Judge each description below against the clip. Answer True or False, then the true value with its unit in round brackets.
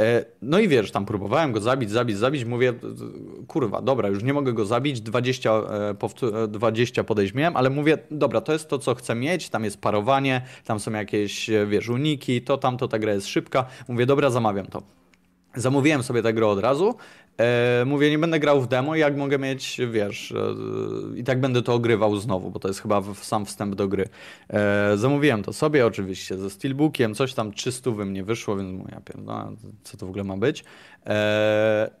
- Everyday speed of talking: False (200 wpm)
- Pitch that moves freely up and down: False (4.3 semitones)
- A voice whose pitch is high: False (115 Hz)